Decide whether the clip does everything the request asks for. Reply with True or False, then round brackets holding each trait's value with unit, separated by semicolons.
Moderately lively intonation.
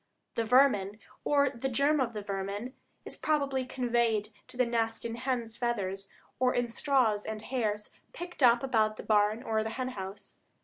True (3.3 semitones)